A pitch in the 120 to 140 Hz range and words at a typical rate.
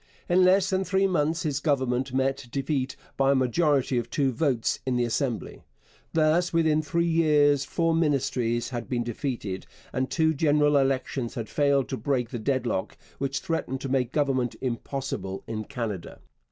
Yes: low, 135 Hz; average, 165 wpm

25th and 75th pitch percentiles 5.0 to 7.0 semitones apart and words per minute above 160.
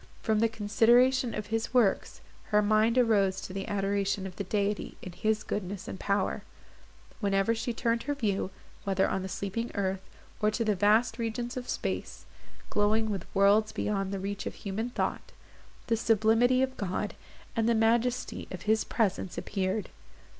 No: narrow, 2.6 semitones; average, 170 wpm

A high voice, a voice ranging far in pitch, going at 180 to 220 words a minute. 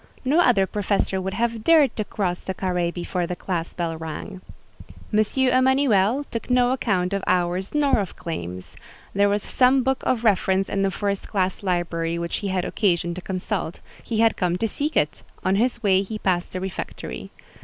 No: high, 195 Hz; average, 4.4 semitones; average, 185 wpm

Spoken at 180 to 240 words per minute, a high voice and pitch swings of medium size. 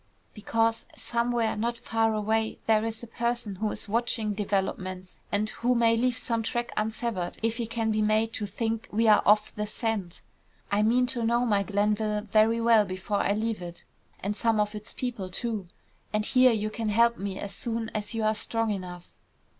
No: average, 195 wpm; high, 220 Hz; narrow, 1.7 semitones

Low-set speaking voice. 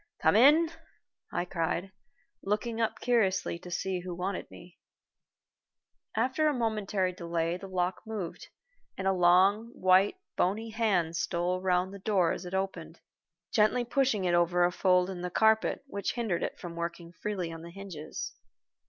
No: high, 190 Hz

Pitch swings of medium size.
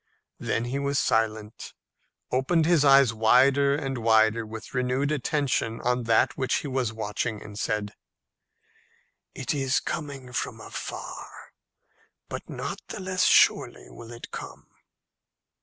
Yes: average, 3.8 semitones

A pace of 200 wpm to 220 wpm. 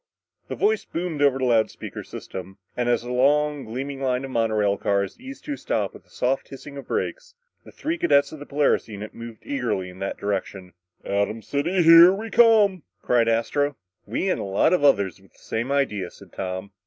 Yes: fast, 205 wpm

